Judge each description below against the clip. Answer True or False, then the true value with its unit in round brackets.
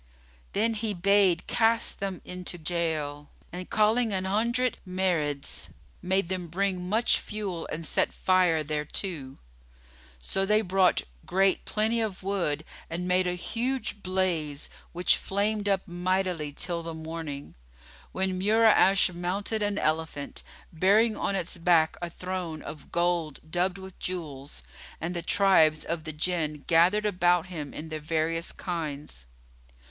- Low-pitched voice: False (180 Hz)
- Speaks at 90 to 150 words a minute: True (140 wpm)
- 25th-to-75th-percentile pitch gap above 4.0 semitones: False (3.4 semitones)